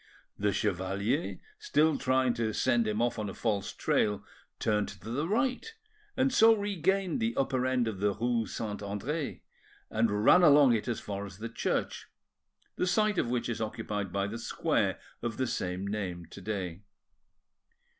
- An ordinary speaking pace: Yes, average, 170 wpm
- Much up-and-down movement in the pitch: Yes, wide, 6.1 semitones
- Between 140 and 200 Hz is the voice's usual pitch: No, low, 115 Hz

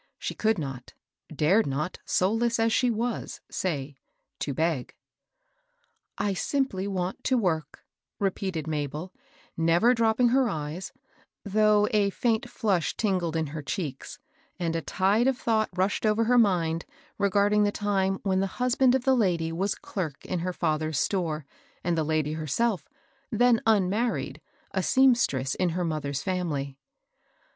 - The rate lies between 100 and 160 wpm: Yes, average, 150 wpm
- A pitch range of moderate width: No, wide, 5.7 semitones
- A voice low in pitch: No, high, 190 Hz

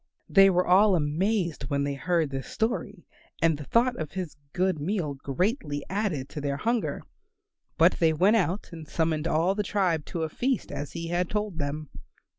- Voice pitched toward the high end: No, medium, 170 Hz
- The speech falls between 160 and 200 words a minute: Yes, average, 185 wpm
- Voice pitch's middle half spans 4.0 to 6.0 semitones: Yes, average, 4.7 semitones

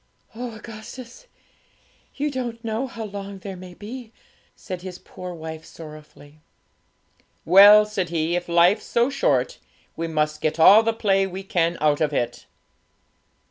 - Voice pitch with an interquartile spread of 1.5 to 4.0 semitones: No, average, 5.2 semitones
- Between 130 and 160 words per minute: Yes, average, 145 wpm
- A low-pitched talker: No, high, 190 Hz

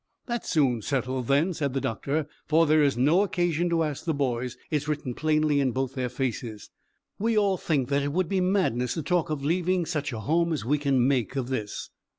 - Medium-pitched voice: Yes, medium, 145 Hz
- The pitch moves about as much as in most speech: Yes, average, 4.3 semitones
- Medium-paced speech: No, fast, 215 wpm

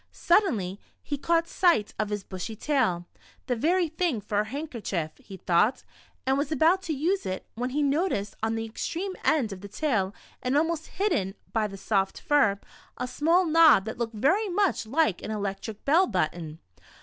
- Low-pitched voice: No, very high, 250 Hz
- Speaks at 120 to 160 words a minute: No, average, 185 wpm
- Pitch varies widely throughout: Yes, wide, 8.0 semitones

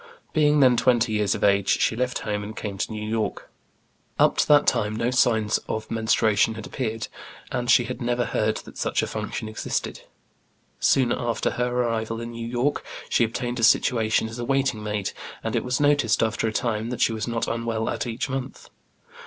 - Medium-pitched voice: No, low, 115 Hz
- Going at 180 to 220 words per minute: Yes, average, 200 wpm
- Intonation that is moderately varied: No, narrow, 2.1 semitones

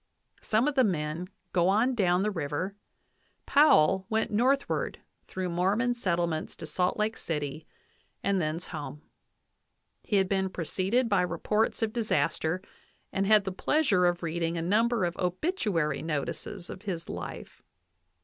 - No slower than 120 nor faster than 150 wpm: Yes, average, 145 wpm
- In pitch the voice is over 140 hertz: Yes, medium, 185 Hz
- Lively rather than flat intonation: No, average, 4.2 semitones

